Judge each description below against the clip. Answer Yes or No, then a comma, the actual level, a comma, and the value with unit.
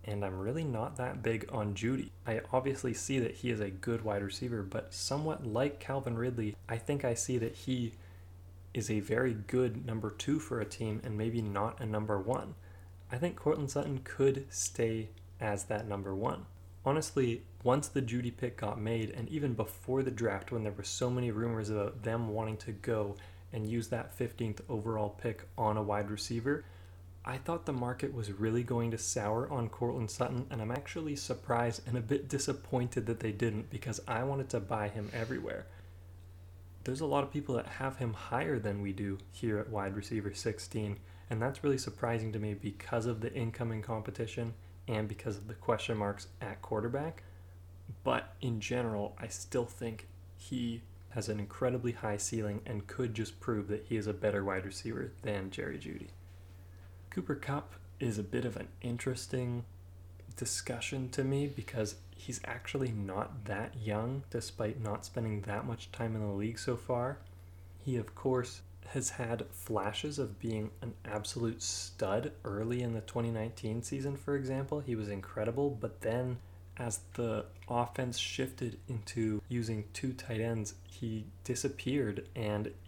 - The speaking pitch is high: No, low, 110 Hz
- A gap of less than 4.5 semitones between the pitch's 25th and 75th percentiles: Yes, average, 3.5 semitones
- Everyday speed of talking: Yes, average, 175 wpm